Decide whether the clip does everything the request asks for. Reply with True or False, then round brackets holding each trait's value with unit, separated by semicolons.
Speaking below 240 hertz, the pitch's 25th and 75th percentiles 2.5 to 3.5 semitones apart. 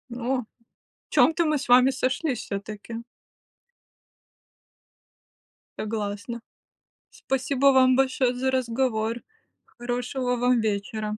False (245 Hz; 2.8 semitones)